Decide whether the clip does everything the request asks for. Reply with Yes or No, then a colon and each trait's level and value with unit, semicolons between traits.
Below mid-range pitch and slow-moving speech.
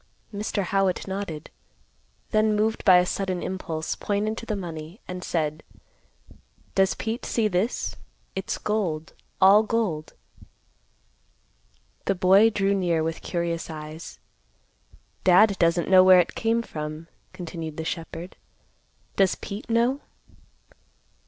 No: medium, 185 Hz; slow, 120 wpm